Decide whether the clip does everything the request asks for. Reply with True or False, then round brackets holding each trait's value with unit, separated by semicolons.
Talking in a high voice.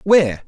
False (160 Hz)